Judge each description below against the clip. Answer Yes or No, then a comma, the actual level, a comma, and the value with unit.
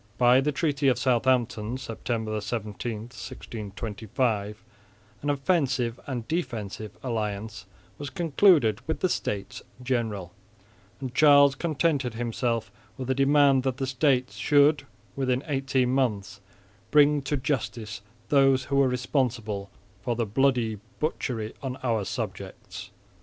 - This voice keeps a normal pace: No, slow, 120 wpm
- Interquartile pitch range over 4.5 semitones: No, average, 3.7 semitones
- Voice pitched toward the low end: Yes, low, 125 Hz